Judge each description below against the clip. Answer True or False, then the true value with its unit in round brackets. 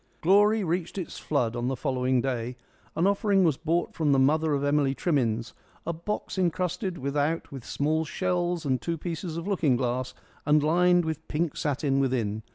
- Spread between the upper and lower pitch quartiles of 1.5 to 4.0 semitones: False (4.6 semitones)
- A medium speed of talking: True (175 wpm)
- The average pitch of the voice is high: False (155 Hz)